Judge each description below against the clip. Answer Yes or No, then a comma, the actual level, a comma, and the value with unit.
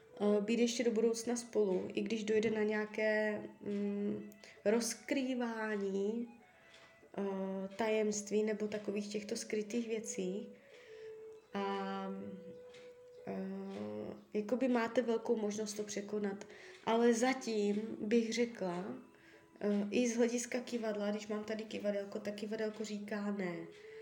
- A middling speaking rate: No, slow, 100 wpm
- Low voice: No, high, 215 Hz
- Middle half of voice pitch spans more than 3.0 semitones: No, narrow, 2.4 semitones